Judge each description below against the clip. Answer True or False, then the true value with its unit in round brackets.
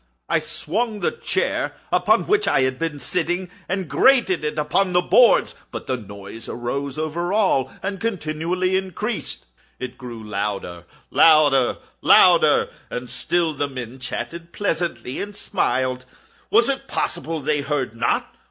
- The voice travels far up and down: True (6.4 semitones)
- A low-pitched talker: False (155 Hz)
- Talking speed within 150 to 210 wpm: False (135 wpm)